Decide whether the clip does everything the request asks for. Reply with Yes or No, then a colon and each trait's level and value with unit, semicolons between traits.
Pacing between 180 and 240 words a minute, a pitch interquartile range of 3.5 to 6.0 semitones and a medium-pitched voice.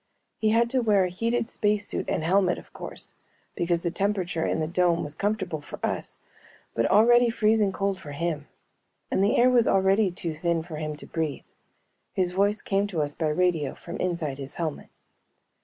Yes: average, 190 wpm; average, 4.4 semitones; medium, 180 Hz